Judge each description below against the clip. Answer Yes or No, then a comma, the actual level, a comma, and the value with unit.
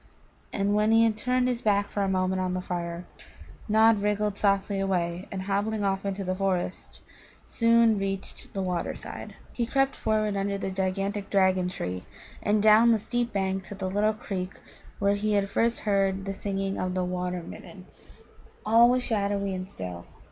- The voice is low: No, high, 200 Hz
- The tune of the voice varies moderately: No, narrow, 2.2 semitones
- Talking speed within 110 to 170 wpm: No, average, 180 wpm